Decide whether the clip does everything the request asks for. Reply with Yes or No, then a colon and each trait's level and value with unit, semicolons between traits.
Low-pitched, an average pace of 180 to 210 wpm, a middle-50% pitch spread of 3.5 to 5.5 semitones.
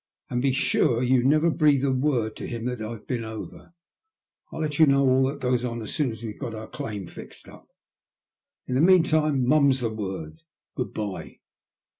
Yes: low, 125 Hz; average, 200 wpm; average, 4.0 semitones